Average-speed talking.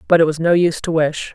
No: fast, 315 wpm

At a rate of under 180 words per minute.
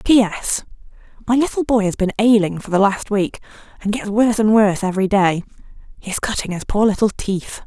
No: average, 195 wpm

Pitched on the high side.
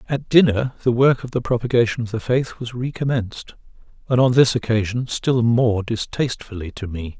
No: low, 120 Hz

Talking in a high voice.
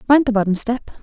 Yes: high, 230 Hz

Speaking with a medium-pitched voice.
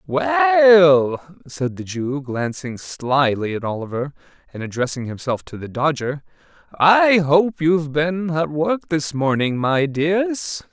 Yes: medium, 155 Hz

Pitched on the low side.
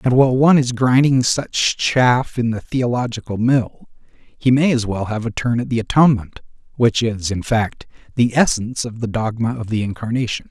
Yes: low, 120 Hz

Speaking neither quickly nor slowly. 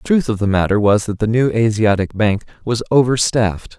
No: fast, 220 wpm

